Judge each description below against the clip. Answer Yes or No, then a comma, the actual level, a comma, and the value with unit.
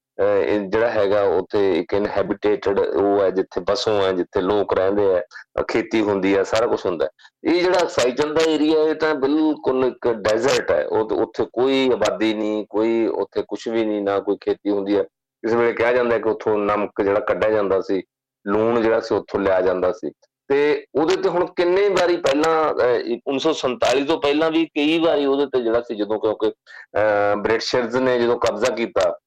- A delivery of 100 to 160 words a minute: No, average, 185 wpm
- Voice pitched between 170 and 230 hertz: No, low, 135 Hz